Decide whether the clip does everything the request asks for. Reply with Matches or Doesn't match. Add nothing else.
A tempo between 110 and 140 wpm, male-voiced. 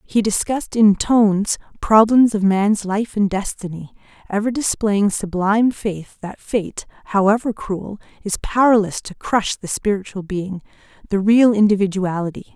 Doesn't match